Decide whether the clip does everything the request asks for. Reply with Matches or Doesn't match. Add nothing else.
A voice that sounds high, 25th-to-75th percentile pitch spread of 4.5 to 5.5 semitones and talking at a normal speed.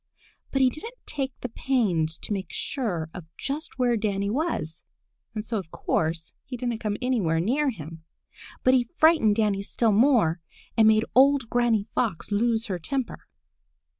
Matches